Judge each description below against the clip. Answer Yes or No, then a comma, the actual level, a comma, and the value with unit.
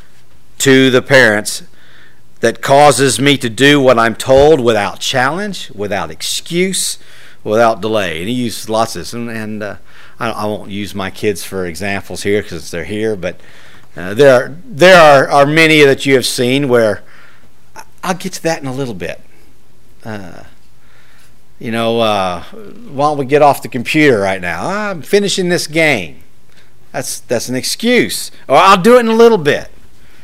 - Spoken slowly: No, average, 175 wpm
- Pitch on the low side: Yes, low, 120 Hz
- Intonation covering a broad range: Yes, wide, 6.0 semitones